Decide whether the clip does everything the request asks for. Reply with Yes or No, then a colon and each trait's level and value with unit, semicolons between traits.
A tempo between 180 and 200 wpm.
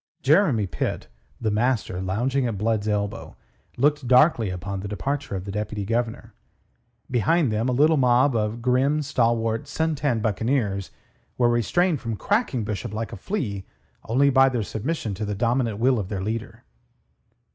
No: average, 160 wpm